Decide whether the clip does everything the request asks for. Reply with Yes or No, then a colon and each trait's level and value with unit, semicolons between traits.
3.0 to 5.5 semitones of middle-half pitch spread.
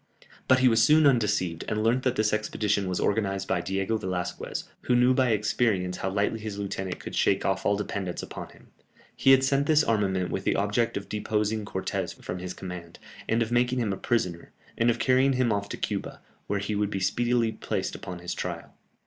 Yes: average, 3.9 semitones